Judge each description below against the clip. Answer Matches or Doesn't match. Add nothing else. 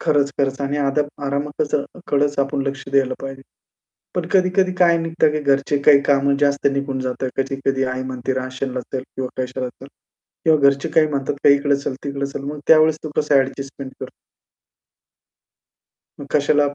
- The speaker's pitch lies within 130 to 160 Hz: Matches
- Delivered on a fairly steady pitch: Matches